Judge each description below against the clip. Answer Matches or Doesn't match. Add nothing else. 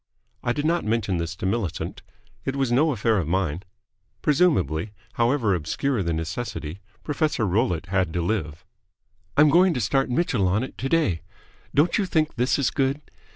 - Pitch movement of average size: Doesn't match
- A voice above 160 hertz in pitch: Doesn't match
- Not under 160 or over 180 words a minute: Matches